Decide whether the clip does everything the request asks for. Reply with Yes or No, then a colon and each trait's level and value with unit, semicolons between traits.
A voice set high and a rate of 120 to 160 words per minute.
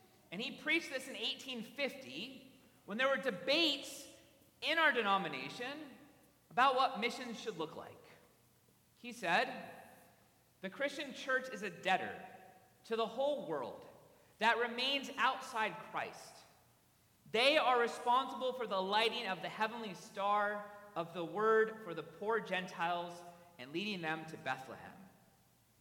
Yes: high, 225 Hz; slow, 135 wpm